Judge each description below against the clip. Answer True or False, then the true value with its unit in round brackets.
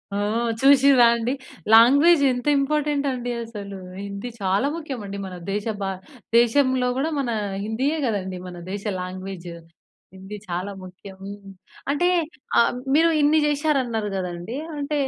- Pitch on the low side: False (235 Hz)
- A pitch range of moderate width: False (6.1 semitones)